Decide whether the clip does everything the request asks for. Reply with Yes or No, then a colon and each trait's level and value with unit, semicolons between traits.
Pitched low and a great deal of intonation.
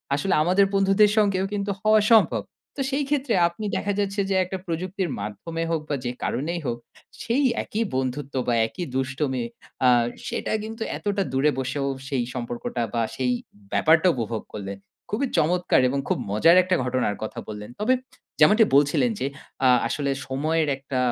No: medium, 160 Hz; wide, 7.4 semitones